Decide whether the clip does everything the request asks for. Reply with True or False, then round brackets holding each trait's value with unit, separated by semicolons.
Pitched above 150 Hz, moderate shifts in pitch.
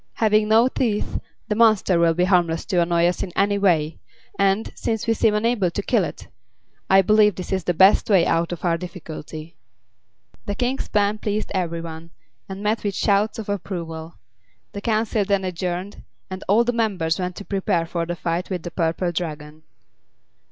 True (190 Hz; 3.6 semitones)